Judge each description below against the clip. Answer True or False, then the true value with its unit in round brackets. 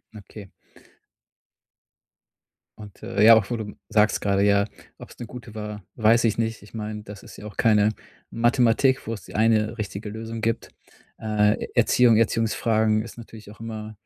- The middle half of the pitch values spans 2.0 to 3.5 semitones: False (1.4 semitones)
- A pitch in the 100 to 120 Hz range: True (110 Hz)